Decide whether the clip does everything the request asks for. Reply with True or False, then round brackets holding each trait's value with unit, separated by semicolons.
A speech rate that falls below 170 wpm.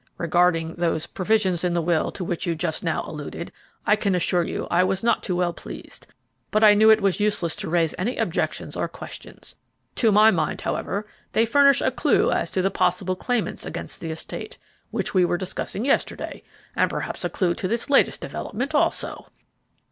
False (195 wpm)